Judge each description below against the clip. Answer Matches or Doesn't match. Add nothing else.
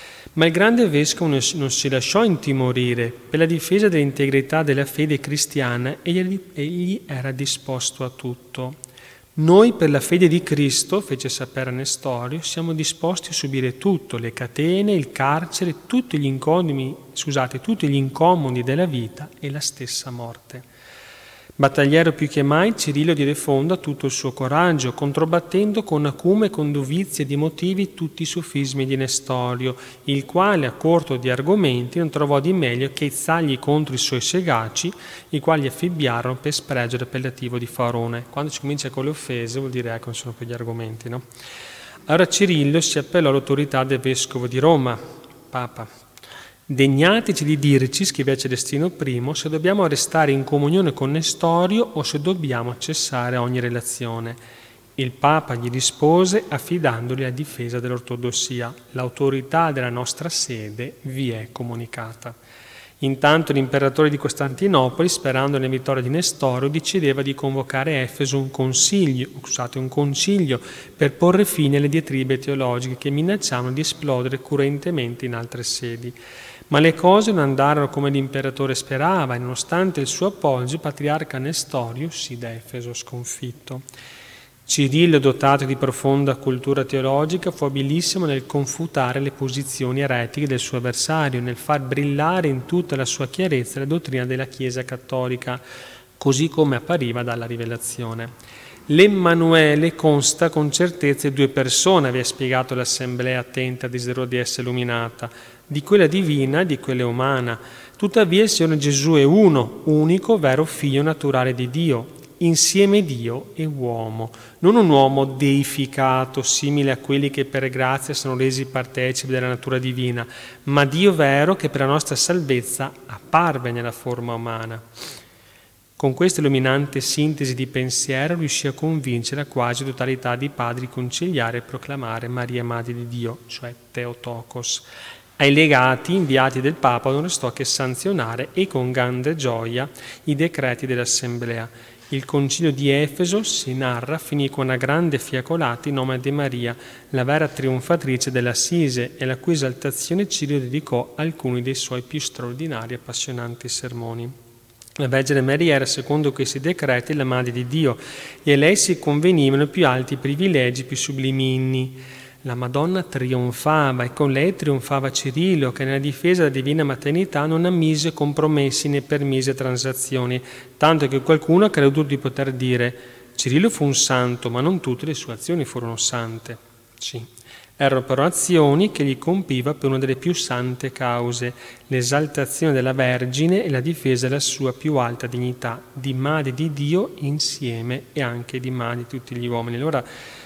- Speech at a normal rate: Matches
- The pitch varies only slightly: Doesn't match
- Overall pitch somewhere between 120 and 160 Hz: Matches